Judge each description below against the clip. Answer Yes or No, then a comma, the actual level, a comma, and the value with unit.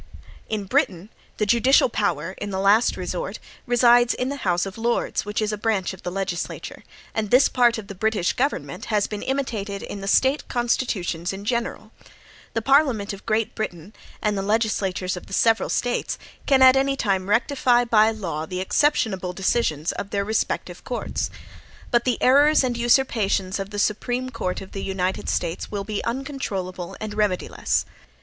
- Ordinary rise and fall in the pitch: Yes, average, 3.9 semitones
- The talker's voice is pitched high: Yes, high, 215 Hz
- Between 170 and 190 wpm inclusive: Yes, average, 175 wpm